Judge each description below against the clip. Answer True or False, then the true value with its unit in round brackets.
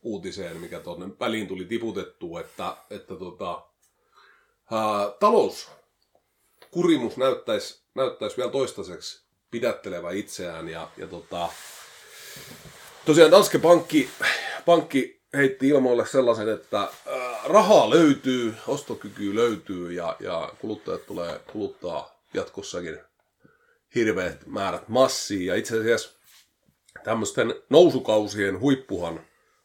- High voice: False (130 Hz)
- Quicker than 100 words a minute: False (95 wpm)